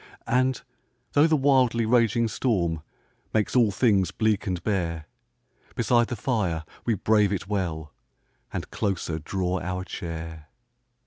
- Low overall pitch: Yes, low, 100 Hz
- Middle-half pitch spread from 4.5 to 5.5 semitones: Yes, average, 5.1 semitones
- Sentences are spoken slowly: Yes, slow, 130 wpm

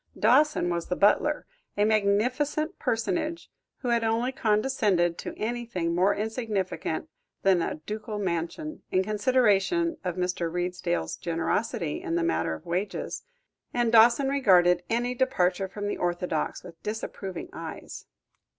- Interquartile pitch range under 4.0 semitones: No, average, 5.3 semitones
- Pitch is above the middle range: Yes, high, 205 Hz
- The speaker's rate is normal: No, slow, 130 wpm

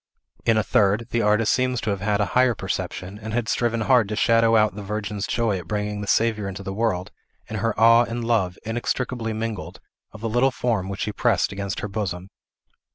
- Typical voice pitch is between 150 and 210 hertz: No, low, 110 Hz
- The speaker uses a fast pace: Yes, fast, 215 wpm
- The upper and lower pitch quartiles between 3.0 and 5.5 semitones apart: No, narrow, 2.5 semitones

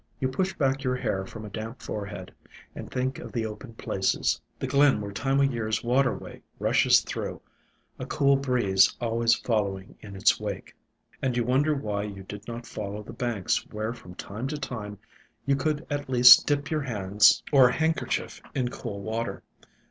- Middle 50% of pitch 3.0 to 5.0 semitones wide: Yes, average, 4.5 semitones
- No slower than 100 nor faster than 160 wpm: No, average, 180 wpm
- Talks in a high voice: No, low, 120 Hz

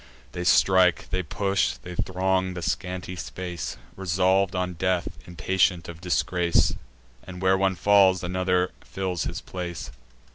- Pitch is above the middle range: No, very low, 90 Hz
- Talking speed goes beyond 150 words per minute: No, slow, 135 wpm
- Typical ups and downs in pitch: No, narrow, 1.1 semitones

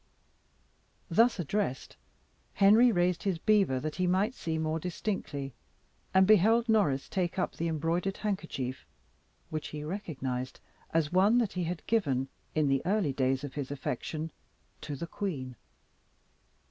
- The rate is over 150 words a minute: No, average, 140 wpm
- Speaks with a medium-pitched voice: Yes, medium, 170 Hz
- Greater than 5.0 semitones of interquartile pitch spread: Yes, wide, 5.6 semitones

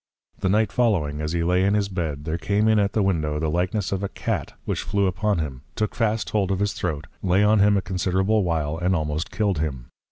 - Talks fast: Yes, fast, 235 wpm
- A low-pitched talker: Yes, very low, 95 Hz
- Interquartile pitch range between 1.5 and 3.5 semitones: No, average, 4.3 semitones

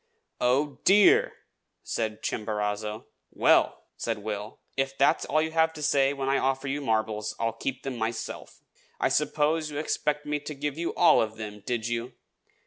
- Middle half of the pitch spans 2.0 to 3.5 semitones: No, average, 5.0 semitones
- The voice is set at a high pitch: No, low, 135 Hz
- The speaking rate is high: No, average, 170 wpm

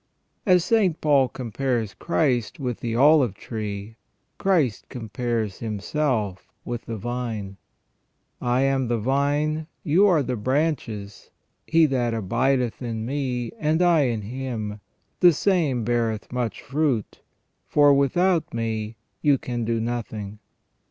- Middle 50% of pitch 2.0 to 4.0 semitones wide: No, average, 4.5 semitones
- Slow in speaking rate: Yes, slow, 125 wpm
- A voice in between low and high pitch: No, low, 125 Hz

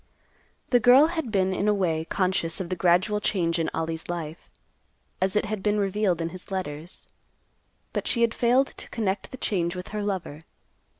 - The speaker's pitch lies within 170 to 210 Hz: Yes, high, 190 Hz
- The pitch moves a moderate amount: Yes, average, 3.7 semitones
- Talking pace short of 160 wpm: No, average, 185 wpm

